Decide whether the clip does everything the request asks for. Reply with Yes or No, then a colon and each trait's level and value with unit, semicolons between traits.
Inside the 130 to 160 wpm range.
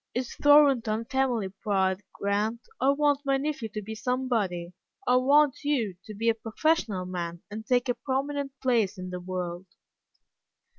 Yes: average, 155 wpm